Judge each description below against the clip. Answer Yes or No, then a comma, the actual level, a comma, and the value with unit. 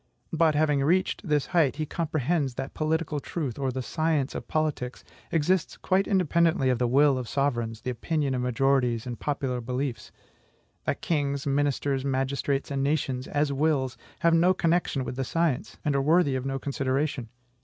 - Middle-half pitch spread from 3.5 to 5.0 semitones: No, average, 3.1 semitones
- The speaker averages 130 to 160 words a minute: No, average, 170 wpm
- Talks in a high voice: No, medium, 140 Hz